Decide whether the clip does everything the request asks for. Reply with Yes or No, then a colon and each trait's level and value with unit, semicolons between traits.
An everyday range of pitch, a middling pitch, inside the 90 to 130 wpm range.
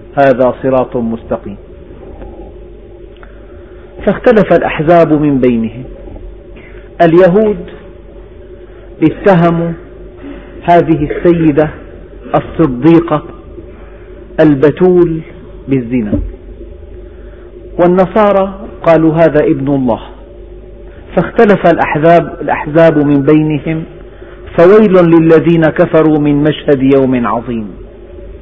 No: average, 3.5 semitones; medium, 160 Hz; slow, 65 wpm